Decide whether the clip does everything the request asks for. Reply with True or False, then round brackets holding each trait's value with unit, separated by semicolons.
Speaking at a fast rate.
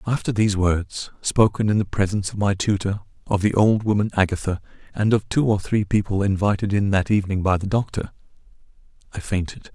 False (185 wpm)